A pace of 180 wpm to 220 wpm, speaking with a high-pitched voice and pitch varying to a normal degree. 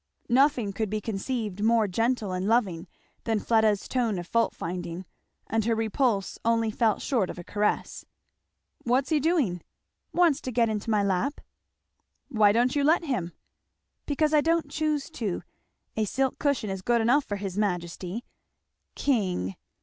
No: average, 155 wpm; high, 225 Hz; average, 4.7 semitones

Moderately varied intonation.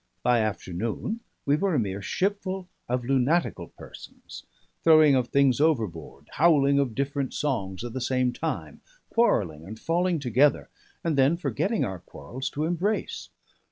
No: wide, 6.0 semitones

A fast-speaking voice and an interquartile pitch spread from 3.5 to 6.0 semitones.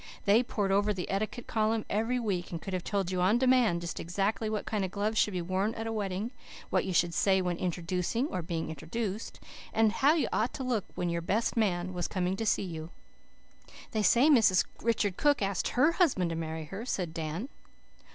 Yes: fast, 210 wpm; average, 4.0 semitones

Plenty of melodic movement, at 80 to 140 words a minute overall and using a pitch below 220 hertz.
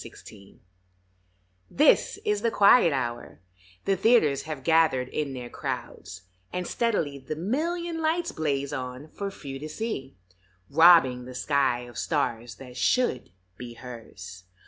Yes: wide, 7.6 semitones; slow, 135 wpm; medium, 140 Hz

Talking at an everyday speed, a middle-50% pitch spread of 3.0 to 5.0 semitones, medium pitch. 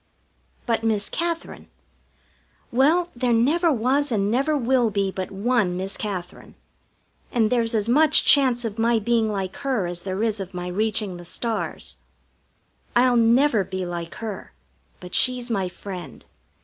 No: average, 150 wpm; average, 4.4 semitones; high, 225 Hz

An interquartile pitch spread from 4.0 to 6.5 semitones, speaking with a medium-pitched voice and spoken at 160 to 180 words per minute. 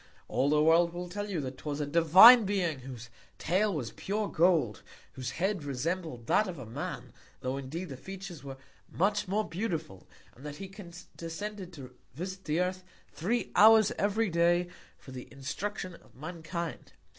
Yes: average, 5.2 semitones; medium, 170 Hz; average, 170 wpm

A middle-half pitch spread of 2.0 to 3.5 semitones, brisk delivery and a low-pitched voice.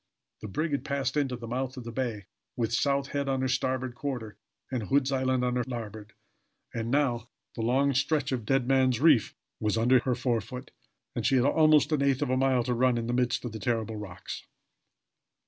Yes: narrow, 2.5 semitones; fast, 210 wpm; low, 125 Hz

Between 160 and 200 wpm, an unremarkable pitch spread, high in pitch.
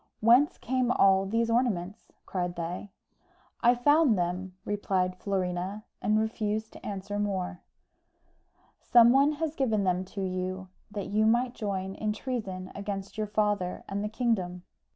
No: average, 145 wpm; average, 3.6 semitones; high, 205 Hz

